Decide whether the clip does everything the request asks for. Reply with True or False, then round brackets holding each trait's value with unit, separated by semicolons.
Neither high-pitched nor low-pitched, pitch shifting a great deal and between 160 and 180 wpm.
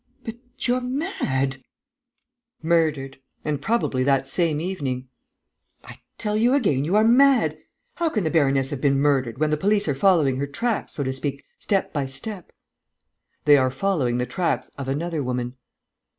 True (150 Hz; 6.7 semitones; 165 wpm)